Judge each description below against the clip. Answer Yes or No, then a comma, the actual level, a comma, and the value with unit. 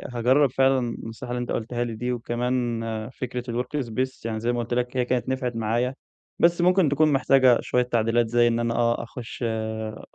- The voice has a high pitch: No, low, 120 Hz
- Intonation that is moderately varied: No, narrow, 1.7 semitones